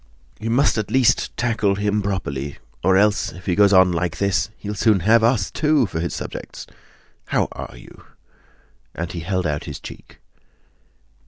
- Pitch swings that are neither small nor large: Yes, average, 3.8 semitones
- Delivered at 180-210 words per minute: No, average, 170 wpm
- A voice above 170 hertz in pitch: No, low, 100 Hz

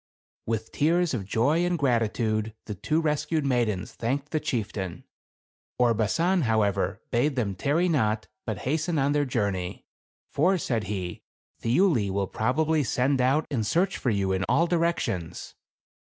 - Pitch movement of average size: No, wide, 6.3 semitones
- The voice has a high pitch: No, low, 125 Hz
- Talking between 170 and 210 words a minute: No, average, 150 wpm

